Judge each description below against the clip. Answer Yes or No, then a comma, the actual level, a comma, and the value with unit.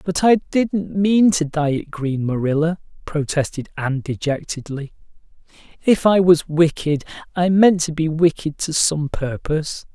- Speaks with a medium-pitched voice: Yes, medium, 160 Hz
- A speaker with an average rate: Yes, average, 145 wpm